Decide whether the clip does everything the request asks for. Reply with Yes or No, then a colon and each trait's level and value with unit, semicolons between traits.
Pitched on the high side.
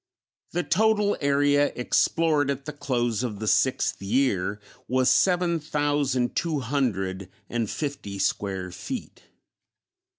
No: low, 135 Hz